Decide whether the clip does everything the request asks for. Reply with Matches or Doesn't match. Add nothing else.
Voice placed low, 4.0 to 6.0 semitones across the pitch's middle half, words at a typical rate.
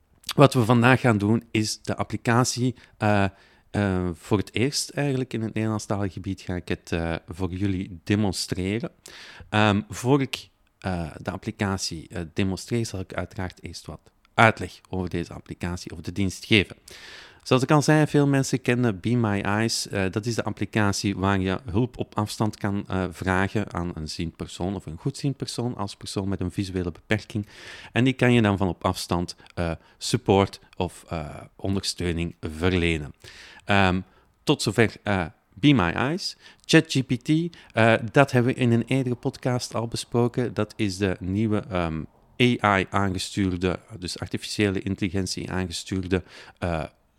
Matches